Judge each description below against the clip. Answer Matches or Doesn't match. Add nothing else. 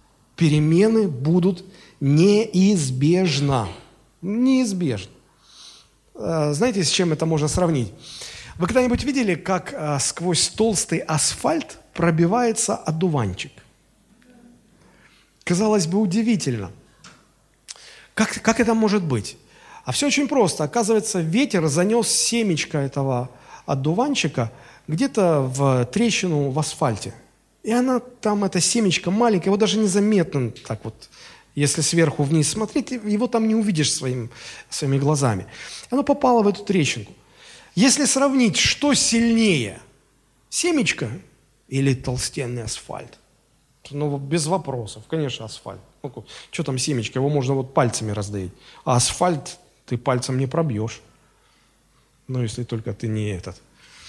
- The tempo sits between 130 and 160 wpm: Doesn't match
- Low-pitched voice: Doesn't match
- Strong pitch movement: Matches